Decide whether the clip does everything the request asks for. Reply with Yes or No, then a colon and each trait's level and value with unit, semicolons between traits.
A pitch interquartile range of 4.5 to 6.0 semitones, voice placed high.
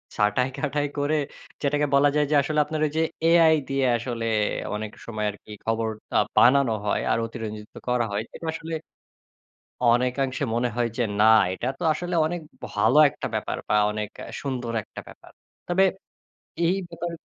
No: average, 5.0 semitones; low, 130 Hz